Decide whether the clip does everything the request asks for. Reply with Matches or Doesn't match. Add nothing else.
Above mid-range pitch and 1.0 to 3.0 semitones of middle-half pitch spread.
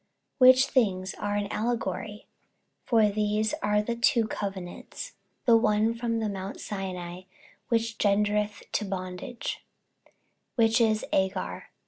Matches